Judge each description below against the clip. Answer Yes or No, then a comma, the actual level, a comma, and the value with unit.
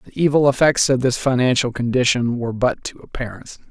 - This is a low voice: Yes, low, 125 Hz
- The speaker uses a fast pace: No, average, 180 wpm